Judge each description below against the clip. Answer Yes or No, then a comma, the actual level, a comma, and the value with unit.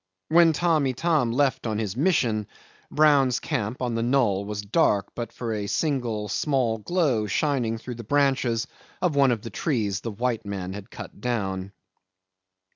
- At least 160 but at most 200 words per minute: Yes, average, 165 wpm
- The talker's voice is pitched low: Yes, low, 120 Hz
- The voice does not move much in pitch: No, average, 4.9 semitones